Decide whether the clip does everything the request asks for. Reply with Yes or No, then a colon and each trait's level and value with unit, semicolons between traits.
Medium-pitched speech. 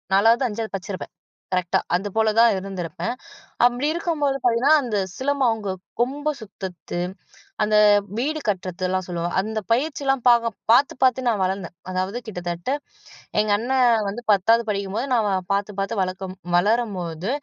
No: high, 215 Hz